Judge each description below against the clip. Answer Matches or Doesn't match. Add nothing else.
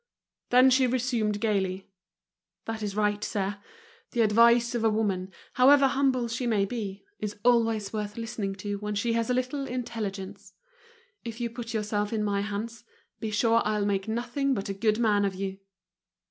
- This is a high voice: Matches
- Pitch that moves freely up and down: Doesn't match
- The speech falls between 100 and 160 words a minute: Doesn't match